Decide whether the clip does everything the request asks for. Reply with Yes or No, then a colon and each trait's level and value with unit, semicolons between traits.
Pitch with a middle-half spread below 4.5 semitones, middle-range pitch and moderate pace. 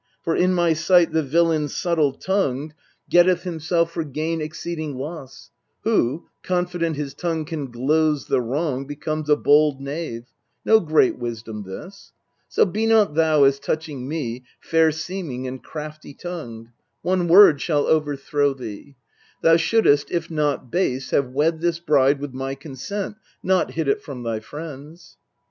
Yes: average, 3.6 semitones; medium, 155 Hz; average, 160 wpm